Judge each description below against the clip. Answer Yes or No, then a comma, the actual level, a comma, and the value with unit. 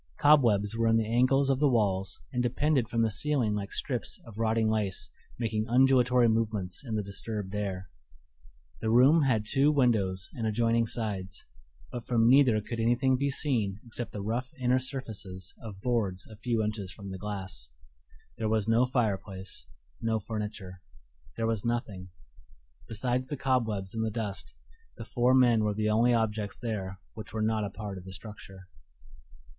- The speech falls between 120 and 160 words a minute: No, average, 170 wpm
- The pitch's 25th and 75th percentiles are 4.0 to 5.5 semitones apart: No, average, 3.1 semitones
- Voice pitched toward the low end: Yes, low, 110 Hz